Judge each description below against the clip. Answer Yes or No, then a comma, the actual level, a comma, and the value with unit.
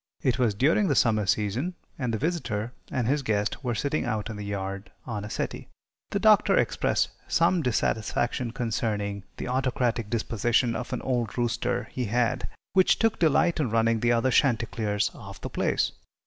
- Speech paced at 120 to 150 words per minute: No, average, 175 wpm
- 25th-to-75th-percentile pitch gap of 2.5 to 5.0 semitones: Yes, average, 3.3 semitones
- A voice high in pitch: No, low, 120 Hz